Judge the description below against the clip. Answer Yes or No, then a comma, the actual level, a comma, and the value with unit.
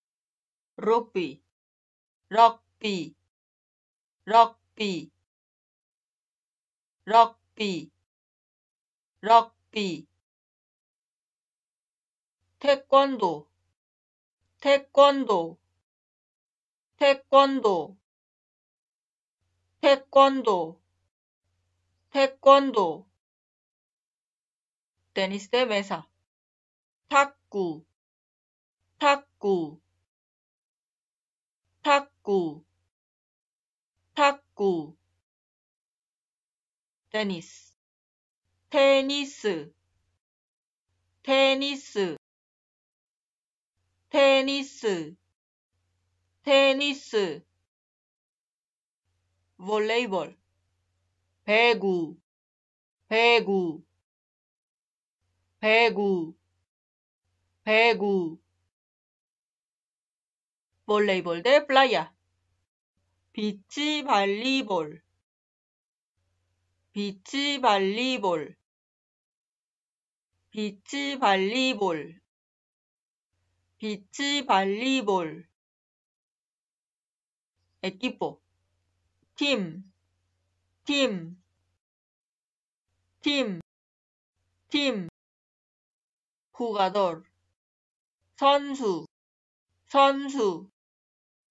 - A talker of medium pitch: Yes, medium, 165 Hz